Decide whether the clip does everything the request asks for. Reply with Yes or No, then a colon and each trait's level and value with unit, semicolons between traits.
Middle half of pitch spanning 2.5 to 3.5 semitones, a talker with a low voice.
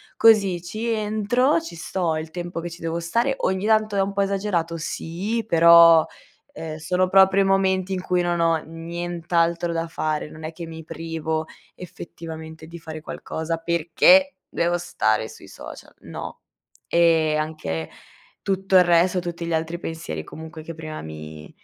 No: average, 2.8 semitones; medium, 170 Hz